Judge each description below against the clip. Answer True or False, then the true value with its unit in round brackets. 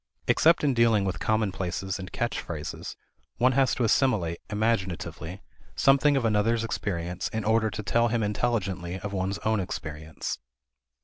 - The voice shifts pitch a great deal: False (4.0 semitones)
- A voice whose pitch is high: False (105 Hz)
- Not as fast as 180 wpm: True (145 wpm)